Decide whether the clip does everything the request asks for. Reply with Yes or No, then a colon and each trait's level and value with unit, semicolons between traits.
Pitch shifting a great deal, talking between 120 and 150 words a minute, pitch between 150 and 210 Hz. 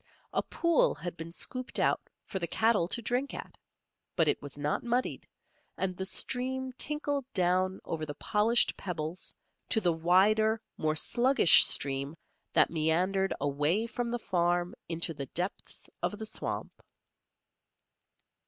Yes: wide, 6.1 semitones; average, 145 wpm; medium, 185 Hz